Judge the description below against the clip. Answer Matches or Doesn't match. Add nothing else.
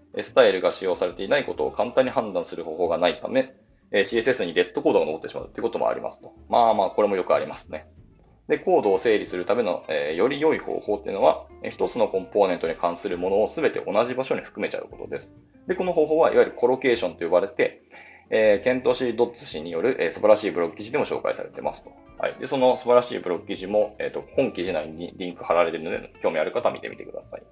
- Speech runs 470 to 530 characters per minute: Matches